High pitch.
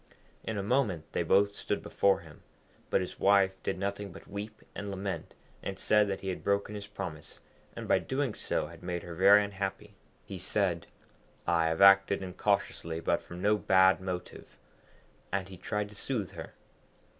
No: low, 100 Hz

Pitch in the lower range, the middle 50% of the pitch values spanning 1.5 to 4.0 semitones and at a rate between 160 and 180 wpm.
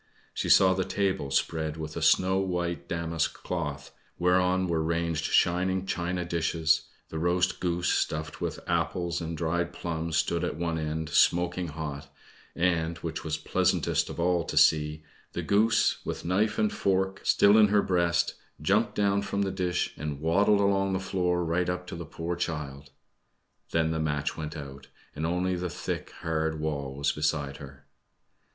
Yes: very low, 85 Hz; narrow, 2.6 semitones; average, 170 wpm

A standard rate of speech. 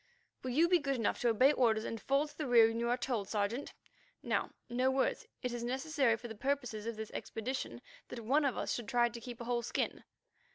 No: fast, 240 wpm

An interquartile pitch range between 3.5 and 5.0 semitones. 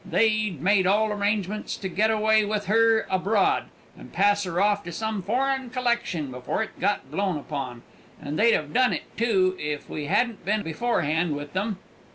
Yes: average, 4.0 semitones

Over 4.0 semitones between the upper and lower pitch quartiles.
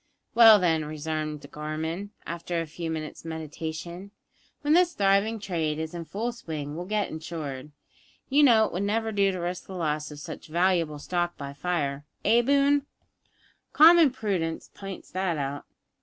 Yes: average, 4.9 semitones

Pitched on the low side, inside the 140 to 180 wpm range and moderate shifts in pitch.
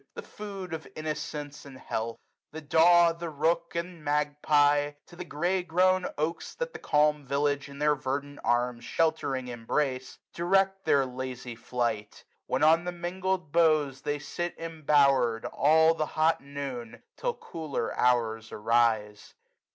No: medium, 150 Hz; average, 145 wpm; average, 4.3 semitones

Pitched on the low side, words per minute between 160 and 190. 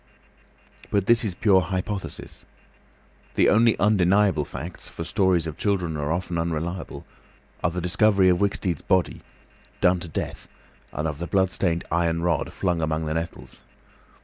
No: very low, 90 Hz; average, 145 wpm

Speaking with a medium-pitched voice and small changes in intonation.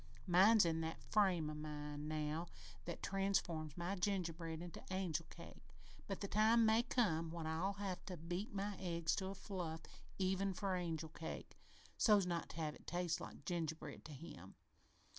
No: medium, 175 Hz; average, 3.4 semitones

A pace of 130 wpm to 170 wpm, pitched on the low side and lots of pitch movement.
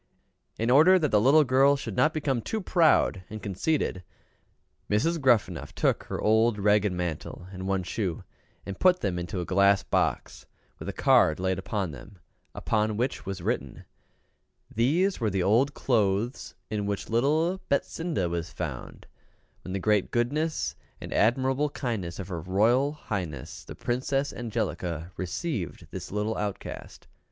Yes: average, 150 wpm; low, 110 Hz; wide, 6.3 semitones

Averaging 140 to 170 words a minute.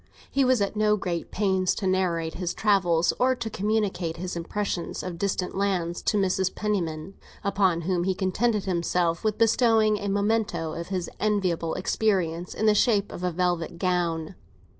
Yes: average, 165 wpm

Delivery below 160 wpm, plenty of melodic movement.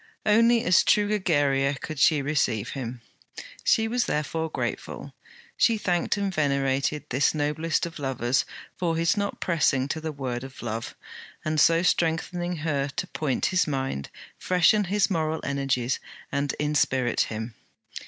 No: average, 145 wpm; average, 4.4 semitones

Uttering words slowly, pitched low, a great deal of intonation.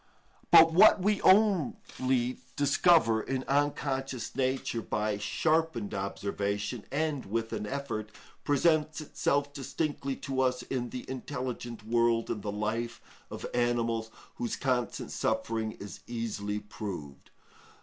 No: slow, 120 wpm; low, 125 Hz; average, 4.3 semitones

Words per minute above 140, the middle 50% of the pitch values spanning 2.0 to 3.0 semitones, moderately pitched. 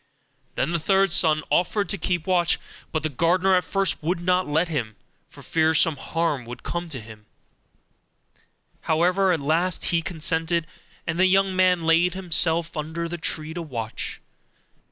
Yes: average, 165 wpm; narrow, 2.4 semitones; medium, 170 Hz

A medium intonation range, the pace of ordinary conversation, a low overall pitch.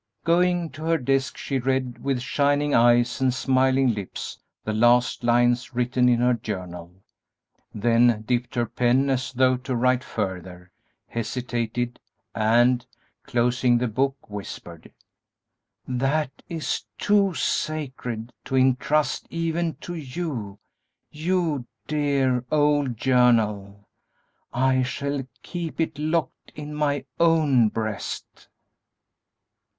No: average, 3.4 semitones; slow, 115 wpm; low, 125 Hz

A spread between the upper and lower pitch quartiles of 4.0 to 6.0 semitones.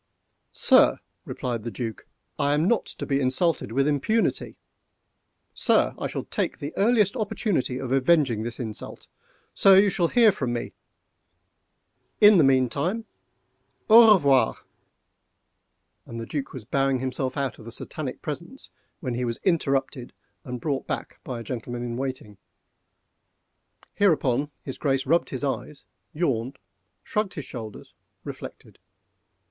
Yes: wide, 5.5 semitones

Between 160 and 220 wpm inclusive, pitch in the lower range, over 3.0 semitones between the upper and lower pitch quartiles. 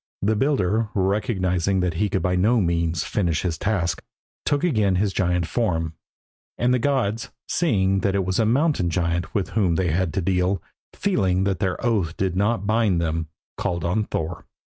Yes: average, 180 wpm; very low, 95 Hz; average, 3.6 semitones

